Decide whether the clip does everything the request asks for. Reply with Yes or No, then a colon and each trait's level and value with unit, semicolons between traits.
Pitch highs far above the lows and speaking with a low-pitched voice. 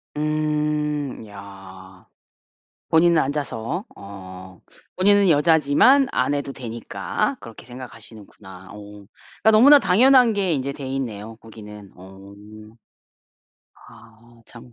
Yes: wide, 6.8 semitones; low, 125 Hz